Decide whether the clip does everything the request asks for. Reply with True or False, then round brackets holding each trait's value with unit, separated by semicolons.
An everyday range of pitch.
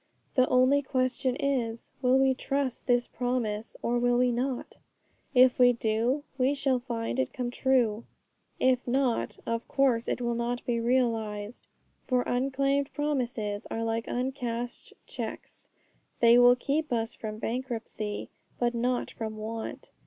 False (2.1 semitones)